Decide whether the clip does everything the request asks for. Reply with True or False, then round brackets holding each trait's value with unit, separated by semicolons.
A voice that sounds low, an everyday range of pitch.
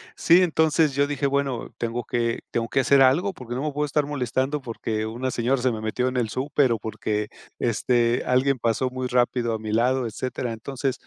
True (125 Hz; 3.0 semitones)